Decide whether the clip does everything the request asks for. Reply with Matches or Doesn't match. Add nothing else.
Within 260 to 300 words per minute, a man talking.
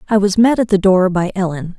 Doesn't match